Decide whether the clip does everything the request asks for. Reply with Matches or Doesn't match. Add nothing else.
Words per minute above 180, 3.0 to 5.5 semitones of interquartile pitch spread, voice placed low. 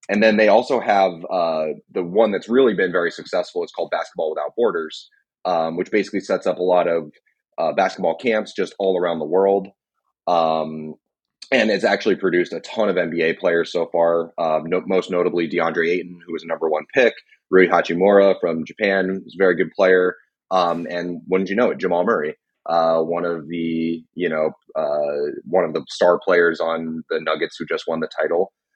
Doesn't match